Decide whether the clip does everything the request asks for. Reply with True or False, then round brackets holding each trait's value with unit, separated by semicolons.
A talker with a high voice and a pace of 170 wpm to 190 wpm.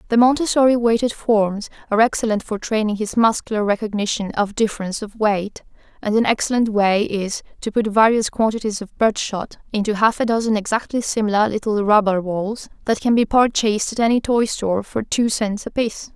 True (215 Hz; 175 wpm)